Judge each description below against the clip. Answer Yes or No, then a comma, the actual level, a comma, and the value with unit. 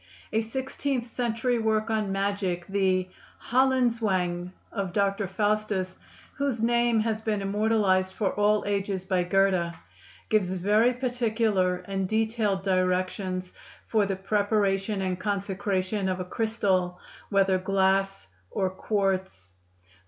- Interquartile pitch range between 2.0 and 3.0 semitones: Yes, average, 2.7 semitones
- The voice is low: No, high, 200 Hz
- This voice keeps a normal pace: No, slow, 115 wpm